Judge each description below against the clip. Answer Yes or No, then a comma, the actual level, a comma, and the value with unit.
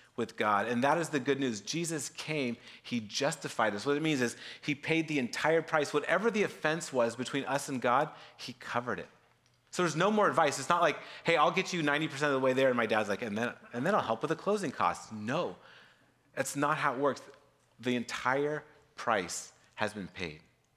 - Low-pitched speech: No, medium, 145 Hz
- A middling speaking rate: No, fast, 220 wpm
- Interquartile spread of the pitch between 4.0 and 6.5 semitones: Yes, average, 4.5 semitones